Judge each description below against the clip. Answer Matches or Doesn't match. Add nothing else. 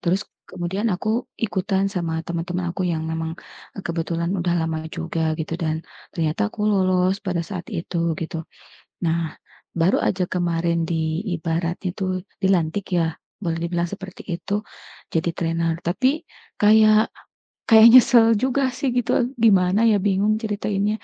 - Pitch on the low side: Doesn't match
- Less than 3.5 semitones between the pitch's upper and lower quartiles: Doesn't match